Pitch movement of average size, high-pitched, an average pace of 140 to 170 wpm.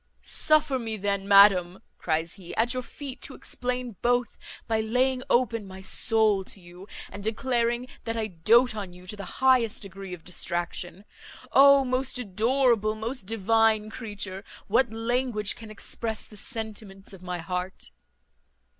Yes: average, 4.0 semitones; high, 220 Hz; average, 150 wpm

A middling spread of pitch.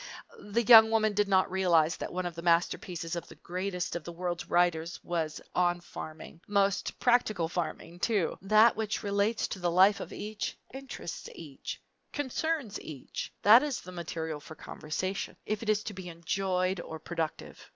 Yes: average, 3.7 semitones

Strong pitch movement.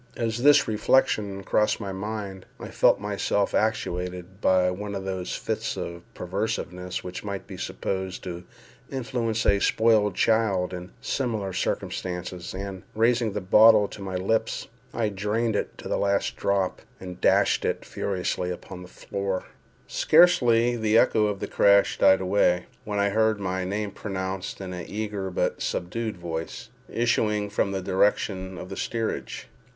No: average, 2.8 semitones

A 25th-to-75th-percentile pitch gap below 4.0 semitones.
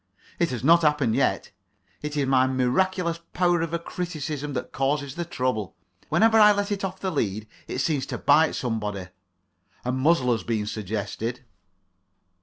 No: wide, 5.5 semitones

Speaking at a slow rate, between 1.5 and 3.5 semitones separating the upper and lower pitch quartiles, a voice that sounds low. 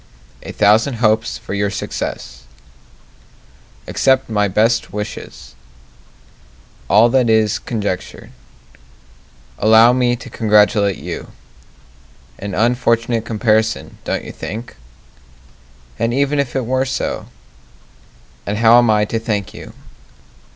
Yes: slow, 110 wpm; narrow, 2.5 semitones; low, 110 Hz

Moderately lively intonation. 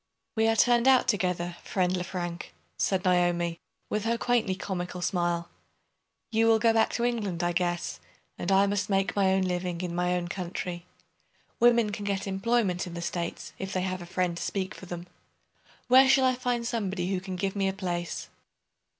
Yes: average, 3.5 semitones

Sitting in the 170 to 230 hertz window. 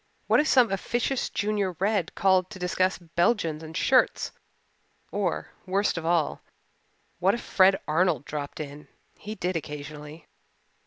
Yes: medium, 185 Hz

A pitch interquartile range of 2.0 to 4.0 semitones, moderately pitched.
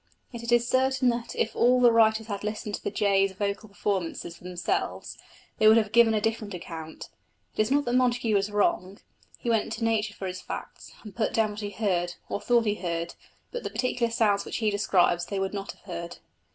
No: average, 2.9 semitones; high, 210 Hz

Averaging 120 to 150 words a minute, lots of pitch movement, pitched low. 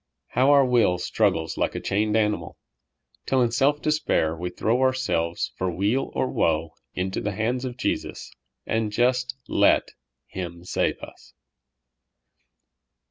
Yes: slow, 135 wpm; wide, 6.1 semitones; low, 110 Hz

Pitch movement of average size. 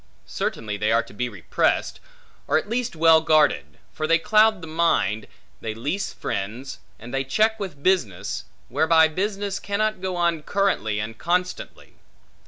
No: wide, 9.0 semitones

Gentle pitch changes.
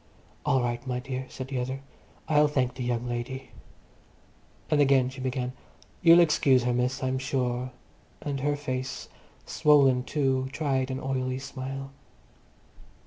Yes: narrow, 1.4 semitones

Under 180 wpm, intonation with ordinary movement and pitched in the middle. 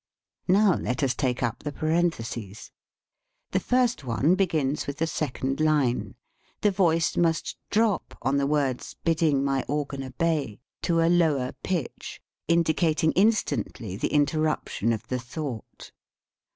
Yes: average, 140 wpm; average, 4.2 semitones; medium, 150 Hz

